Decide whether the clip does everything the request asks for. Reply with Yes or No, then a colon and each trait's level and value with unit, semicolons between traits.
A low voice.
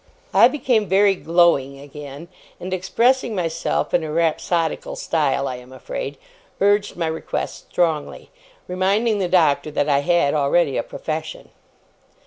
No: medium, 170 Hz